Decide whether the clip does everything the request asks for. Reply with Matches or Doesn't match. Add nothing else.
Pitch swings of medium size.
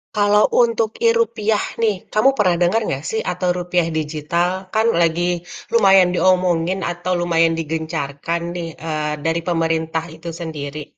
Matches